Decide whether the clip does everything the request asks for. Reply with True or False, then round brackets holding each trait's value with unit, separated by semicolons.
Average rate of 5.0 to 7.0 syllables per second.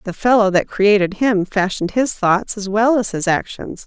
False (4.8 syllables/s)